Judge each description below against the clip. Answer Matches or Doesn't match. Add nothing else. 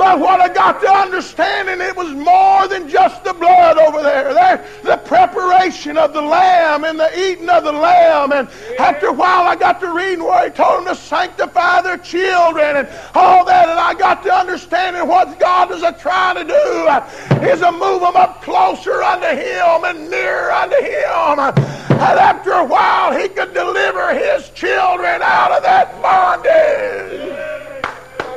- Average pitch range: Doesn't match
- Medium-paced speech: Matches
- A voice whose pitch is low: Doesn't match